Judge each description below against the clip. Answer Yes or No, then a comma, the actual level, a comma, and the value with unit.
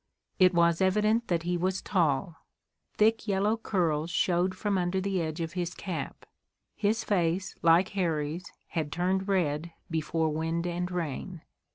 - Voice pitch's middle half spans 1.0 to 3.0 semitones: Yes, average, 2.7 semitones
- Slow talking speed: No, average, 150 wpm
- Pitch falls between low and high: Yes, medium, 175 Hz